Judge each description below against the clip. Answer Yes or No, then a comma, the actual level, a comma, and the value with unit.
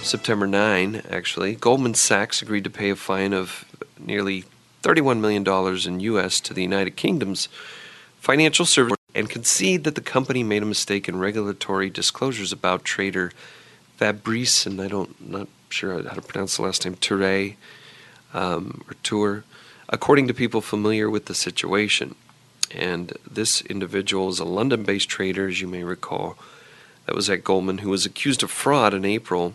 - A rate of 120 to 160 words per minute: No, average, 170 wpm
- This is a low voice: Yes, low, 100 Hz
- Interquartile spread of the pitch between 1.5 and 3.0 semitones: Yes, narrow, 2.6 semitones